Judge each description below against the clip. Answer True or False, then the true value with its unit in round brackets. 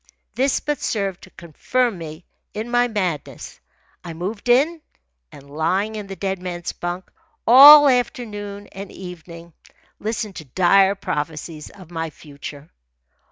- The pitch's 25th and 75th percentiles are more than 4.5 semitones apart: True (5.1 semitones)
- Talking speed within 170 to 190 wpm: False (135 wpm)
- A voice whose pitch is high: True (195 Hz)